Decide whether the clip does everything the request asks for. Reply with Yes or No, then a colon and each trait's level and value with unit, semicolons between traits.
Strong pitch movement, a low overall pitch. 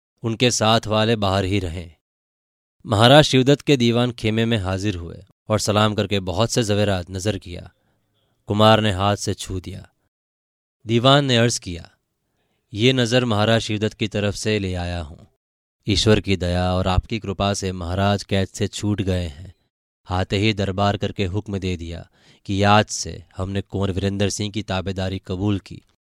No: narrow, 2.6 semitones; low, 100 Hz